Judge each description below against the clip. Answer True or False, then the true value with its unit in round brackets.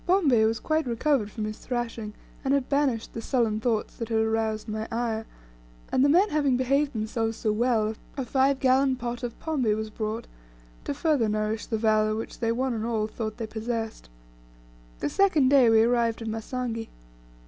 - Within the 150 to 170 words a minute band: False (185 wpm)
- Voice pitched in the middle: False (230 Hz)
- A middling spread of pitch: True (3.1 semitones)